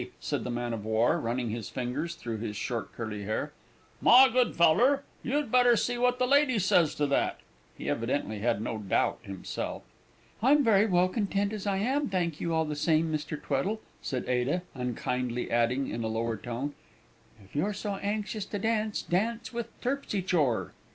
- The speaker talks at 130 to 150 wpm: No, average, 180 wpm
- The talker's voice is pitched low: No, medium, 165 Hz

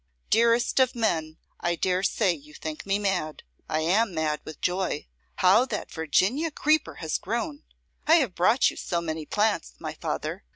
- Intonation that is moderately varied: No, wide, 6.5 semitones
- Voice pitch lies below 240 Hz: Yes, high, 190 Hz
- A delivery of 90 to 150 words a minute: No, average, 170 wpm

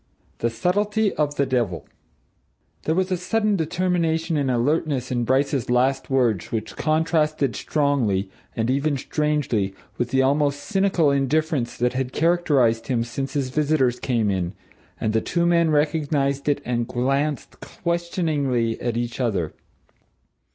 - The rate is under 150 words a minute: Yes, average, 140 wpm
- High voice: No, medium, 140 Hz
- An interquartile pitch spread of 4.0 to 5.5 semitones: Yes, average, 4.6 semitones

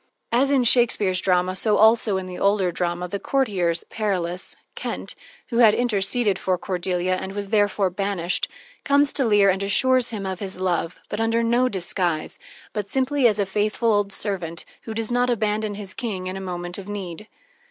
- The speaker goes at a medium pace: Yes, average, 185 wpm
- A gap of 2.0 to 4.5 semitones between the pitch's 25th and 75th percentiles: Yes, average, 3.5 semitones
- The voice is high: Yes, high, 200 Hz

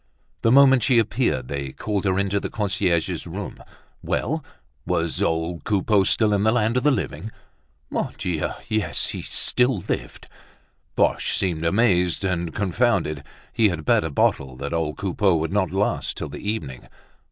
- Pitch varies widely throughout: No, average, 4.8 semitones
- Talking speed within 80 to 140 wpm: No, average, 165 wpm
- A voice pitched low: Yes, very low, 95 Hz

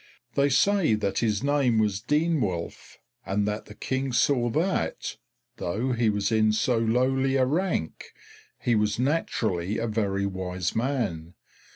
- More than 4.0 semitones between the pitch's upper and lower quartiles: Yes, average, 4.5 semitones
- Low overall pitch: Yes, low, 115 Hz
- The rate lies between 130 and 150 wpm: Yes, average, 145 wpm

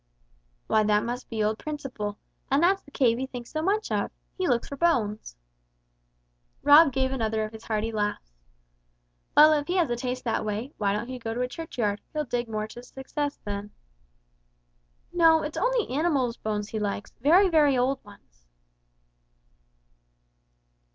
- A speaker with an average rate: Yes, average, 165 wpm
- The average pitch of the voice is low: No, very high, 250 Hz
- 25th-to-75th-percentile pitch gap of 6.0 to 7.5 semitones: No, wide, 5.6 semitones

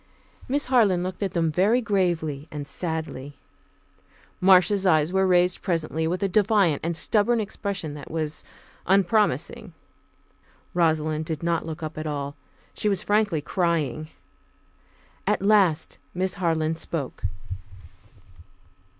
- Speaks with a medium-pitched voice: Yes, medium, 175 Hz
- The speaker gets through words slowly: Yes, slow, 125 wpm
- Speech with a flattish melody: No, average, 3.9 semitones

